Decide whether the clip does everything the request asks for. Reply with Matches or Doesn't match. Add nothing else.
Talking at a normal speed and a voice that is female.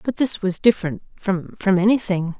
Matches